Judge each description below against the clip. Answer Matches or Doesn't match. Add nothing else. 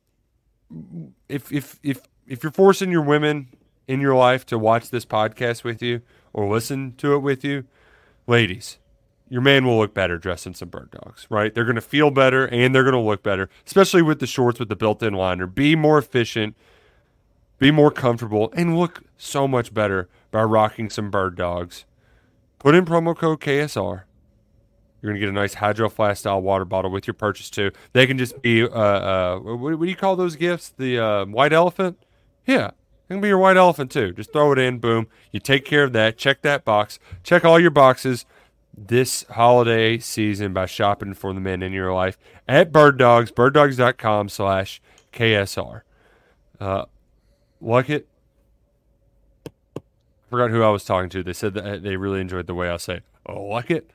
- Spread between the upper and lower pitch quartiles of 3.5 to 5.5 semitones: Matches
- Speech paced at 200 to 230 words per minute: Doesn't match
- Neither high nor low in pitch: Doesn't match